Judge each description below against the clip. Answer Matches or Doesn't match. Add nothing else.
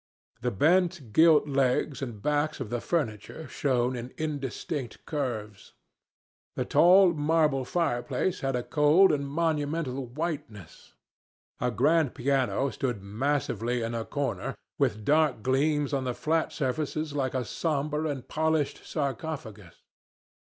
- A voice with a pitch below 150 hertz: Matches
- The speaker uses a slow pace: Matches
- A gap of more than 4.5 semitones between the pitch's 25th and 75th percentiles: Doesn't match